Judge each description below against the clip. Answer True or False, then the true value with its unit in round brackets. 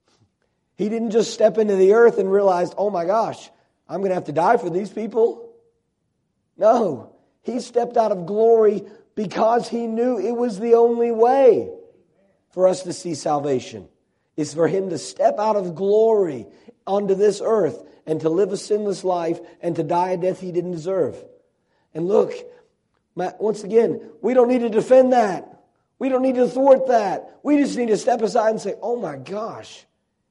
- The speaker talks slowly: False (185 wpm)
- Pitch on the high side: True (215 Hz)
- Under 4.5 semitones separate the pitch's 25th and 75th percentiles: False (4.8 semitones)